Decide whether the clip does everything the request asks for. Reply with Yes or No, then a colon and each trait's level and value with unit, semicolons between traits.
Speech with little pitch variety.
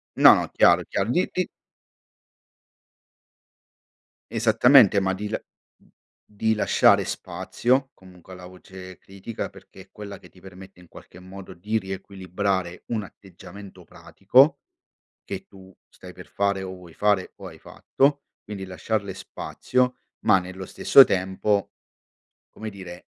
Yes: narrow, 2.3 semitones